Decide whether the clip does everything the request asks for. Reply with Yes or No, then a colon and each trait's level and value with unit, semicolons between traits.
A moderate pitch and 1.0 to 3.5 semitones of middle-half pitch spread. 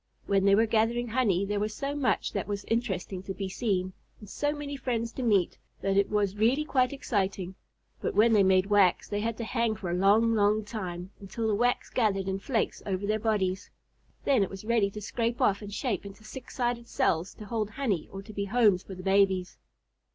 No: high, 210 Hz; average, 3.1 semitones